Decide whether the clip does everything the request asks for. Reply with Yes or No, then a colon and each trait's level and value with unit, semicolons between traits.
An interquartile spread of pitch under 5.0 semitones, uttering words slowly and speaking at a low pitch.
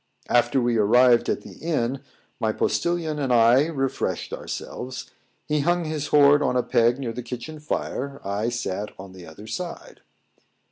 No: average, 4.1 semitones; average, 160 wpm; low, 125 Hz